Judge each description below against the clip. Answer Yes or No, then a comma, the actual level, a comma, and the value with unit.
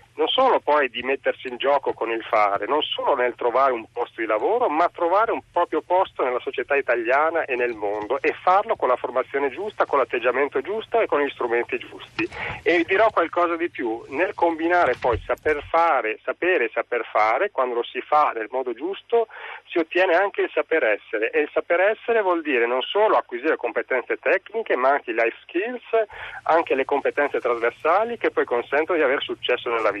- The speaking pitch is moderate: Yes, medium, 180 Hz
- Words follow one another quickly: Yes, fast, 200 wpm